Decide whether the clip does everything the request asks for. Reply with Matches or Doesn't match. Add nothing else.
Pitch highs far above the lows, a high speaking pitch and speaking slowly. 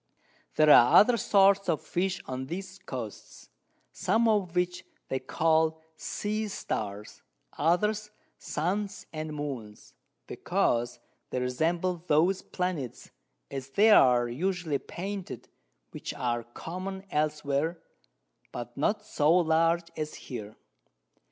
Doesn't match